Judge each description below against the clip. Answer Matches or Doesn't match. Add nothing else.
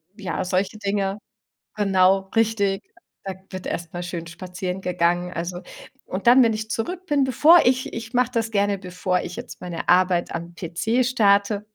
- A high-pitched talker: Matches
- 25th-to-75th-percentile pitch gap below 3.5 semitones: Doesn't match